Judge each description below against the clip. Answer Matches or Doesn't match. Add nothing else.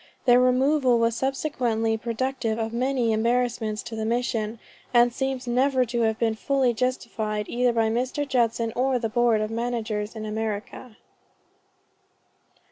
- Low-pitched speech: Doesn't match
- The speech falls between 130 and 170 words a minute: Matches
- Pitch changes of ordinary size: Doesn't match